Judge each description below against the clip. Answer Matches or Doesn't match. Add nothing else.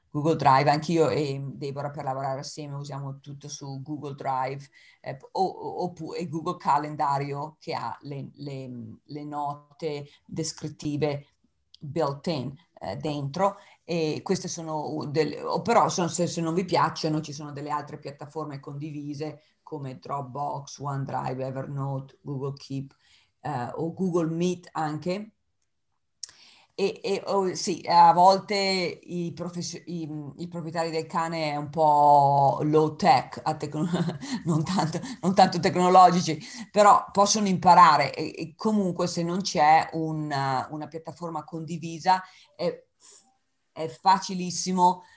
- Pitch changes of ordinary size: Matches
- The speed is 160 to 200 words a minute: Doesn't match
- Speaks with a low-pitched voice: Doesn't match